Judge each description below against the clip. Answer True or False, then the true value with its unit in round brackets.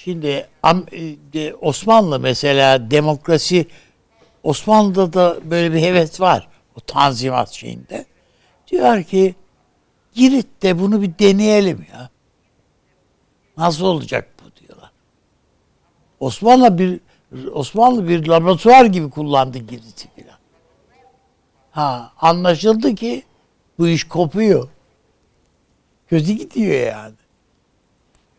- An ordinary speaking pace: False (90 wpm)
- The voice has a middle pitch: True (170 Hz)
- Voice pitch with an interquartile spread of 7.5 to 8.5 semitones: False (5.5 semitones)